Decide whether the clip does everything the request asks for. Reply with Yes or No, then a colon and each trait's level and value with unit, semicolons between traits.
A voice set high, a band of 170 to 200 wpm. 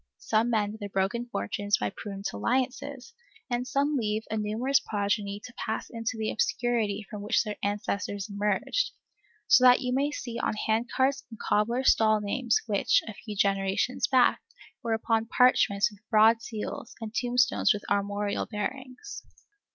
No: high, 220 Hz; average, 155 wpm